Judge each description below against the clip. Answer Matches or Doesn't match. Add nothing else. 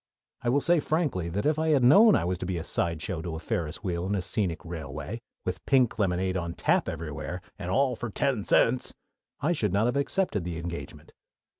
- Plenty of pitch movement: Matches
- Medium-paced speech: Doesn't match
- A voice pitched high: Doesn't match